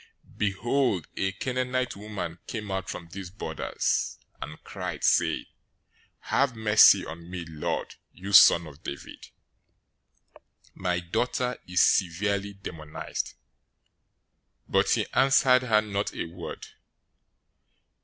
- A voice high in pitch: No, low, 100 Hz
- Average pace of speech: No, slow, 115 wpm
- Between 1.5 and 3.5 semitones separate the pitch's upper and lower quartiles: No, average, 4.4 semitones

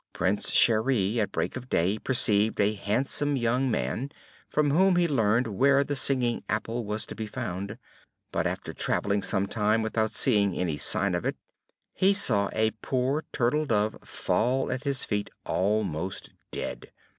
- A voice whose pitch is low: Yes, low, 115 Hz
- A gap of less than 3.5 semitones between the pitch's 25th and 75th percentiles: No, average, 4.4 semitones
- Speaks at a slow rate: No, average, 160 wpm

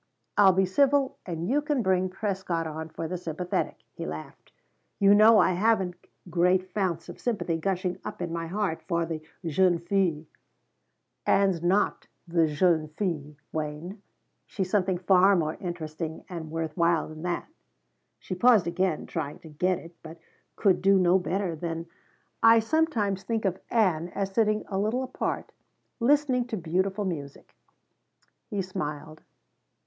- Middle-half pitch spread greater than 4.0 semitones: No, average, 3.3 semitones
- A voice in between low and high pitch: Yes, medium, 180 Hz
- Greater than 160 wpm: No, average, 155 wpm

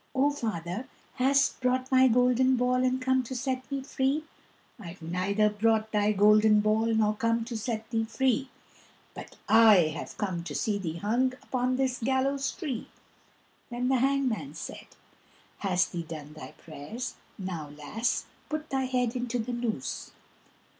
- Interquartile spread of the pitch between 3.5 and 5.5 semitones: Yes, average, 3.8 semitones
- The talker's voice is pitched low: No, high, 230 Hz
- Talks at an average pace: Yes, average, 155 wpm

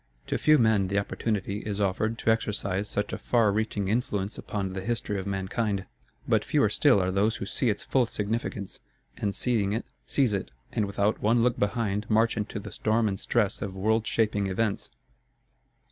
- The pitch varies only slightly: Yes, narrow, 2.3 semitones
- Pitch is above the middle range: No, low, 105 Hz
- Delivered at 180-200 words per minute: Yes, average, 185 wpm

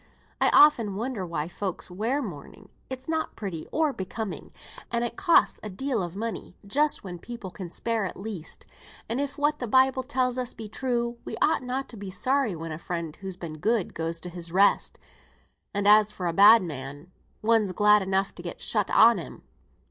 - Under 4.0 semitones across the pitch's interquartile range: No, wide, 5.4 semitones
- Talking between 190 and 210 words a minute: Yes, average, 195 wpm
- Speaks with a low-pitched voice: No, high, 210 Hz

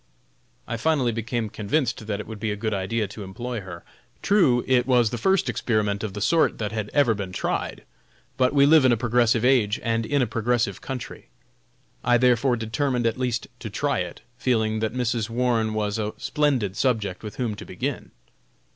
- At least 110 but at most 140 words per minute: No, average, 190 wpm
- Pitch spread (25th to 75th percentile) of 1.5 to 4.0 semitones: Yes, average, 2.8 semitones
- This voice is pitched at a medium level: No, low, 115 Hz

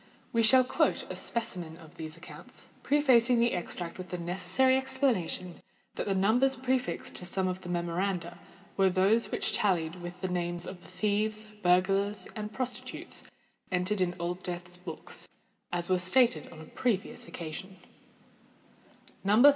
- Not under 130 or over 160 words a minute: Yes, average, 155 wpm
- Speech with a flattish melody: No, average, 4.1 semitones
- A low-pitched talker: No, medium, 185 Hz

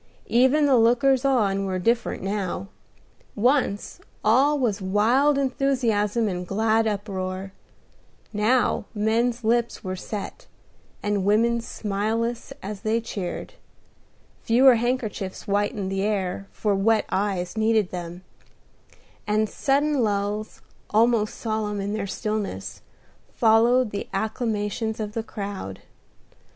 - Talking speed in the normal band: No, slow, 115 wpm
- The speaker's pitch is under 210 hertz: No, high, 215 Hz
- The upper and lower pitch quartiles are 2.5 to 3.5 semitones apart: Yes, average, 2.8 semitones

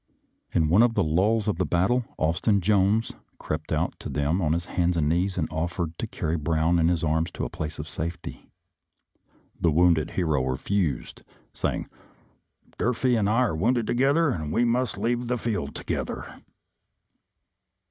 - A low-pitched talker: Yes, very low, 85 Hz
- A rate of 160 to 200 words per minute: Yes, average, 170 wpm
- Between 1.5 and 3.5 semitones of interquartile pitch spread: No, wide, 5.5 semitones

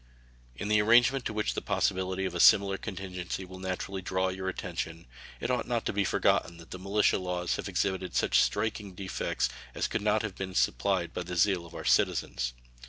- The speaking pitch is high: No, very low, 95 Hz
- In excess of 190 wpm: Yes, average, 200 wpm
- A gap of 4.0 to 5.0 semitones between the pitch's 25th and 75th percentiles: No, narrow, 2.5 semitones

